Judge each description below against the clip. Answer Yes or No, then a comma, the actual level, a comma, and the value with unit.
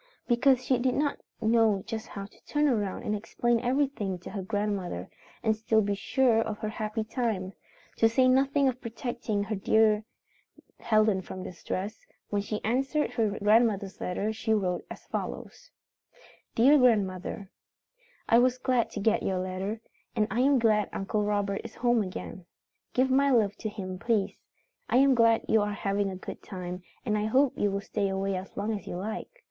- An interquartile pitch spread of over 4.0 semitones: No, average, 3.3 semitones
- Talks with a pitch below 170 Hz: No, high, 215 Hz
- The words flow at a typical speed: Yes, average, 180 wpm